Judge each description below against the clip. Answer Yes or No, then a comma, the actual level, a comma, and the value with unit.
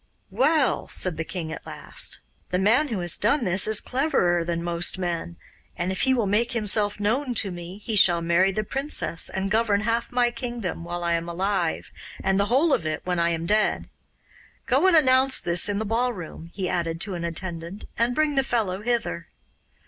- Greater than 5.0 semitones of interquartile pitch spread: Yes, wide, 5.6 semitones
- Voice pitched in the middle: No, high, 200 Hz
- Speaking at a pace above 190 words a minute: Yes, average, 200 wpm